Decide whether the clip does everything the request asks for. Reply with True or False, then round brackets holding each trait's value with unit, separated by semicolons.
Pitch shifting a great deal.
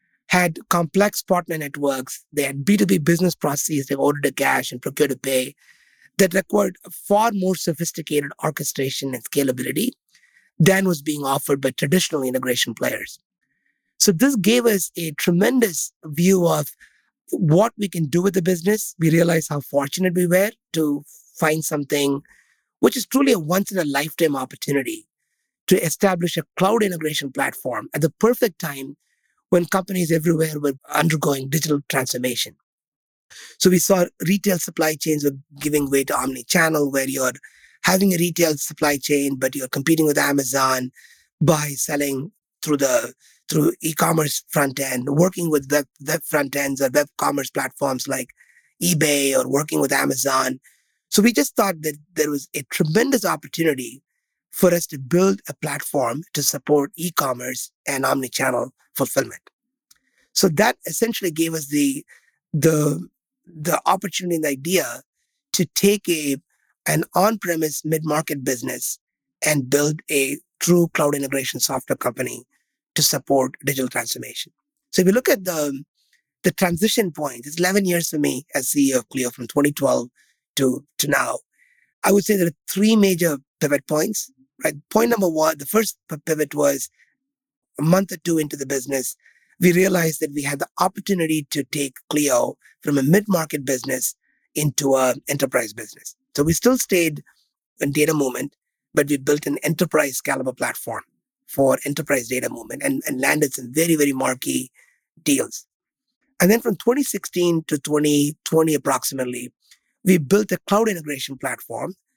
False (4.8 semitones)